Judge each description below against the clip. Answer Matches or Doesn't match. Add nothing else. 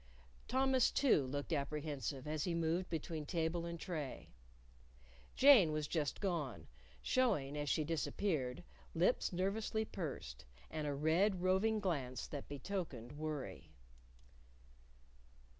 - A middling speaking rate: Doesn't match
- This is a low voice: Doesn't match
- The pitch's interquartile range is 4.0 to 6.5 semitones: Matches